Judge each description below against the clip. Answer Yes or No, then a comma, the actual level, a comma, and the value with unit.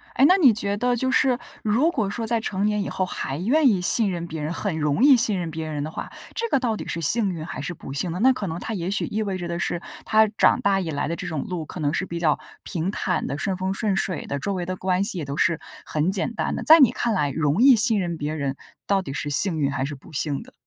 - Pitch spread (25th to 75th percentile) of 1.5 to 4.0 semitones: No, wide, 5.4 semitones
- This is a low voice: No, medium, 185 Hz